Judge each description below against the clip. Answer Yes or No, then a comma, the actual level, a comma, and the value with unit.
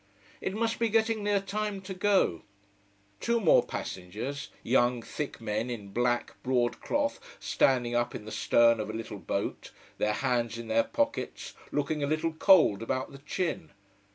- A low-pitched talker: Yes, low, 130 Hz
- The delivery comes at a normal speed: Yes, average, 165 wpm